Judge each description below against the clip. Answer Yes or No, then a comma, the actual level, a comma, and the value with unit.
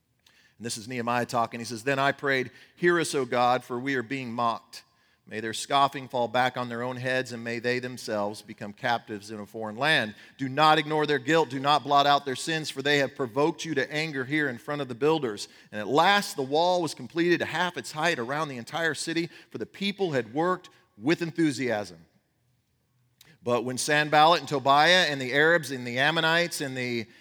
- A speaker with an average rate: No, fast, 215 wpm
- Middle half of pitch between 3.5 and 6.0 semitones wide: Yes, average, 4.3 semitones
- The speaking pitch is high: No, low, 135 Hz